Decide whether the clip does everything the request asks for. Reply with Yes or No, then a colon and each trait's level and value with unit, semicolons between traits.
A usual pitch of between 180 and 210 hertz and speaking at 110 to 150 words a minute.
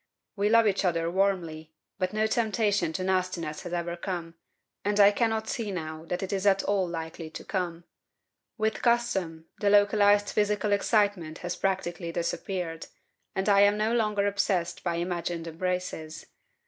No: high, 190 Hz; average, 160 wpm